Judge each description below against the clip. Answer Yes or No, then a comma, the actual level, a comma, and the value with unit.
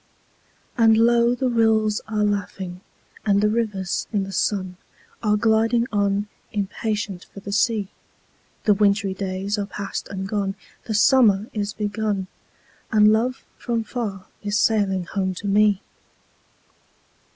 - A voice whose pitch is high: Yes, high, 210 Hz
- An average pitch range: No, narrow, 1.9 semitones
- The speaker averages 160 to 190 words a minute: No, slow, 135 wpm